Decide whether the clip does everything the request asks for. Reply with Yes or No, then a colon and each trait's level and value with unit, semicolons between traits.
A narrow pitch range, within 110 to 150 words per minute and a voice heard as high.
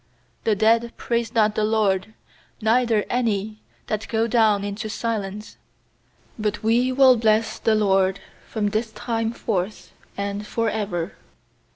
Yes: narrow, 1.8 semitones; slow, 135 wpm; high, 220 Hz